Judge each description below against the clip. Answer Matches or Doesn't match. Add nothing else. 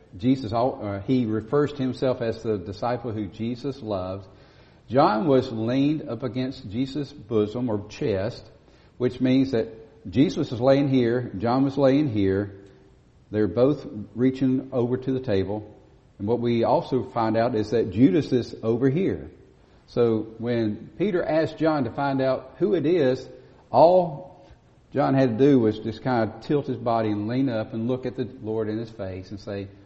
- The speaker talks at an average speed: Matches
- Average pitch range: Matches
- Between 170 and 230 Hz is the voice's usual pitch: Doesn't match